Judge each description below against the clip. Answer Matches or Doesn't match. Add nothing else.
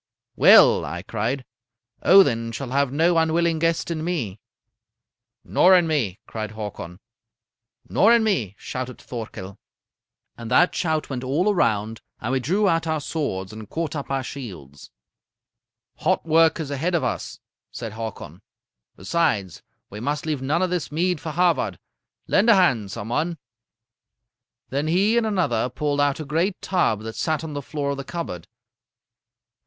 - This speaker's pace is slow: Doesn't match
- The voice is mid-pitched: Matches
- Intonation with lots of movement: Matches